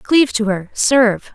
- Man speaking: No, female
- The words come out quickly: No, average, 180 wpm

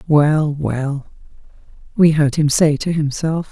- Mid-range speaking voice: Yes, medium, 150 Hz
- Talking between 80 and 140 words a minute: Yes, slow, 135 wpm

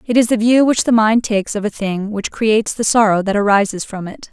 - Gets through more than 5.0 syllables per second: Yes, 5.7 syllables/s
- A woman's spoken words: Yes, female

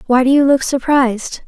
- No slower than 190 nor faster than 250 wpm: Yes, fast, 205 wpm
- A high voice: Yes, very high, 260 Hz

